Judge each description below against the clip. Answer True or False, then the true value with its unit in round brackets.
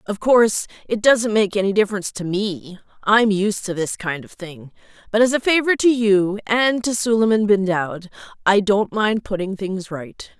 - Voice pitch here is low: False (205 Hz)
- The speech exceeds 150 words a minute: True (180 wpm)